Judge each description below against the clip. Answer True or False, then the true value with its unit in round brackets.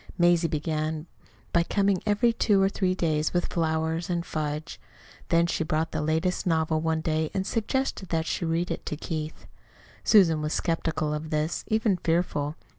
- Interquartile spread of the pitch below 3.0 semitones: True (2.5 semitones)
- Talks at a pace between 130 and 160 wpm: False (170 wpm)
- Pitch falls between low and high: True (165 Hz)